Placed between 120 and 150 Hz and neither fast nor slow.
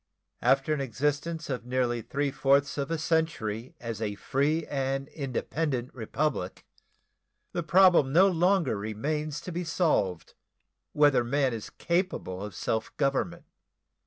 No: medium, 140 Hz; slow, 130 wpm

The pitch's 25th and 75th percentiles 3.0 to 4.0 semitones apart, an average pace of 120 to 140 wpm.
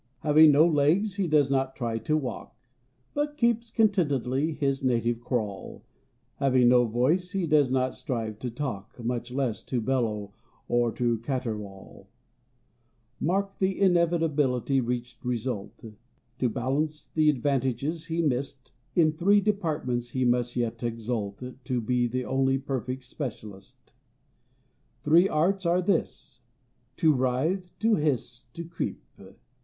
No: average, 4.8 semitones; slow, 135 wpm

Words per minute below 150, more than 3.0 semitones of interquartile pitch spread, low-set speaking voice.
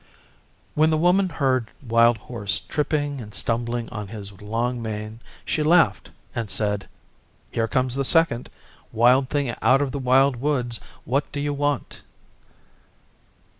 Yes: average, 140 wpm; average, 4.0 semitones; low, 125 Hz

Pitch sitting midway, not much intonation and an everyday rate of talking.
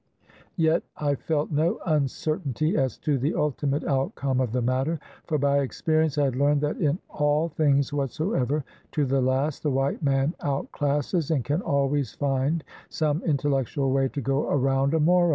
Yes: medium, 145 Hz; narrow, 2.2 semitones; average, 170 wpm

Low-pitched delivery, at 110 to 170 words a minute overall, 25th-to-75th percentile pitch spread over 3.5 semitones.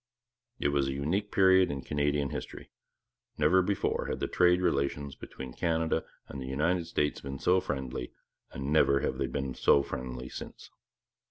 Yes: very low, 70 Hz; average, 165 wpm; average, 4.4 semitones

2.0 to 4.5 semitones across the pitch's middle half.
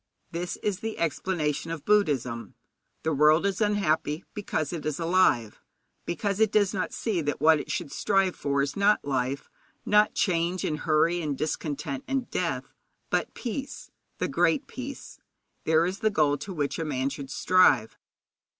No: average, 5.3 semitones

